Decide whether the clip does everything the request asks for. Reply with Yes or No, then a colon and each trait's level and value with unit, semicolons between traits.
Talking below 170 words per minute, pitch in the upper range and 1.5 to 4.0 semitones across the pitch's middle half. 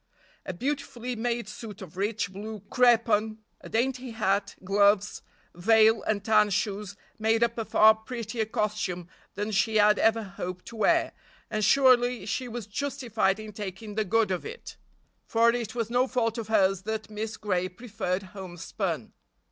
Yes: average, 160 wpm; high, 215 Hz; narrow, 2.5 semitones